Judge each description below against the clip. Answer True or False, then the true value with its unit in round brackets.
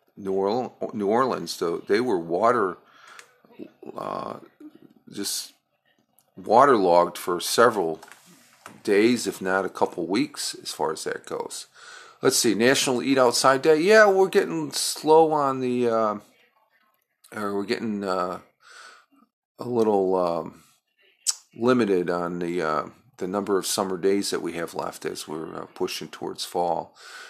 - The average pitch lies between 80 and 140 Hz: True (135 Hz)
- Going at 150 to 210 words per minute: False (135 wpm)